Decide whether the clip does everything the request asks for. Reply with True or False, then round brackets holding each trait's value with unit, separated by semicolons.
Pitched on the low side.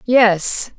False (220 Hz)